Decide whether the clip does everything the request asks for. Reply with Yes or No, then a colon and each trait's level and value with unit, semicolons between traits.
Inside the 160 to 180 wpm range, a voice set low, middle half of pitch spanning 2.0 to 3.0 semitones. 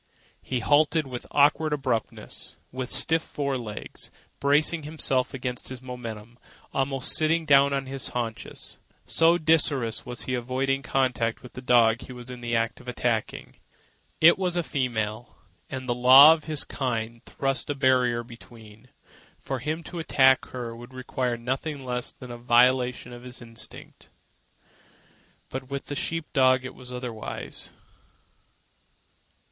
No: average, 150 wpm; low, 130 Hz; narrow, 2.5 semitones